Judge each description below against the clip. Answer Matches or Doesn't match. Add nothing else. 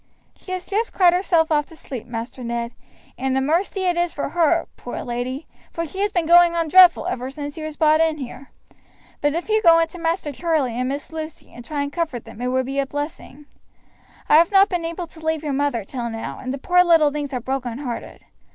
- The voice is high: Matches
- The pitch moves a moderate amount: Matches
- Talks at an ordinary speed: Doesn't match